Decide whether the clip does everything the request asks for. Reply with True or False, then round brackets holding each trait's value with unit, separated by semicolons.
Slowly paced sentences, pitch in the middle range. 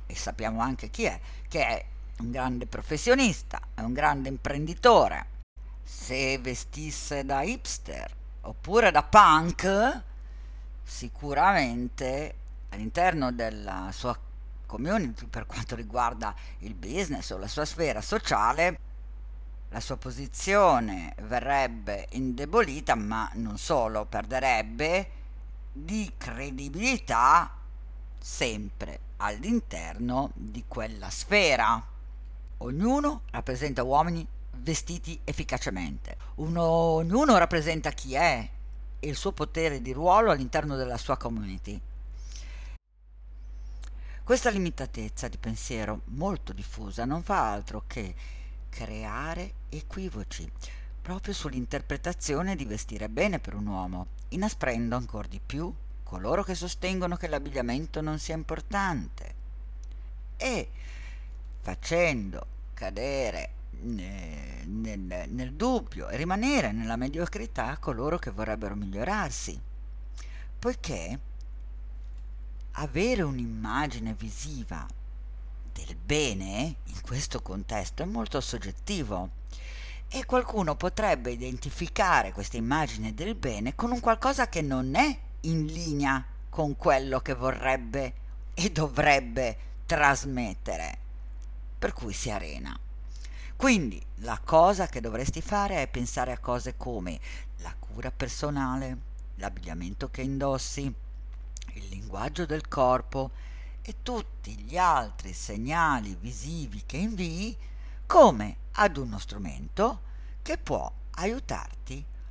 False (105 wpm; 120 Hz)